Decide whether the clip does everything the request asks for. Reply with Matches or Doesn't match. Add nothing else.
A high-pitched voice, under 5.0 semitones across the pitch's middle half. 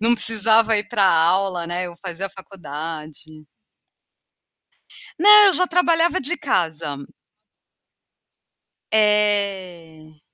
Doesn't match